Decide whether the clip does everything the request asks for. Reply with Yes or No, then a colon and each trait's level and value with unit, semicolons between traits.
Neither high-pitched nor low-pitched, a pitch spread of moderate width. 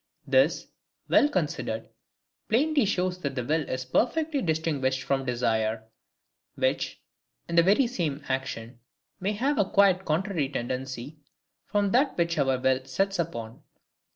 No: medium, 160 Hz; wide, 7.2 semitones